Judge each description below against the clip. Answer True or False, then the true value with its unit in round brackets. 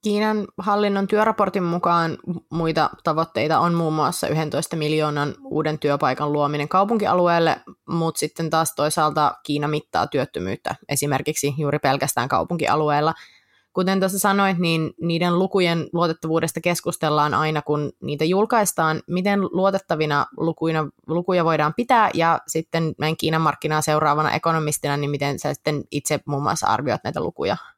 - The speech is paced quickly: False (130 wpm)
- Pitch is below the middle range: False (160 Hz)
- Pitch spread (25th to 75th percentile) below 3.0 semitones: True (2.6 semitones)